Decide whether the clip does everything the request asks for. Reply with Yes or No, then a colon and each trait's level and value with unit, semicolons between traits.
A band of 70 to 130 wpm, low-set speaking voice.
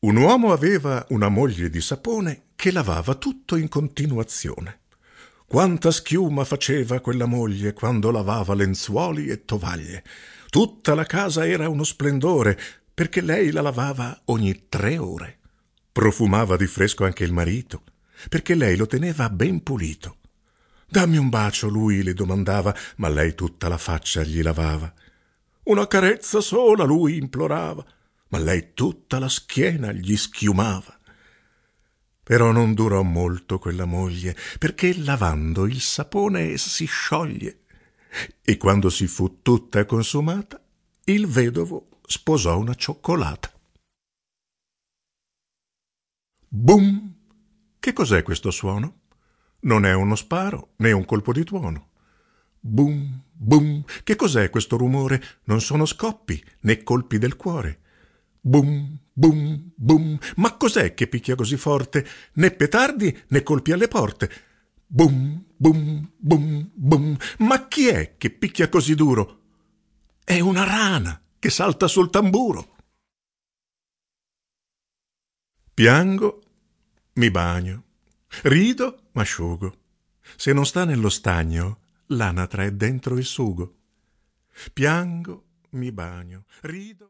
Yes: average, 120 wpm; low, 125 Hz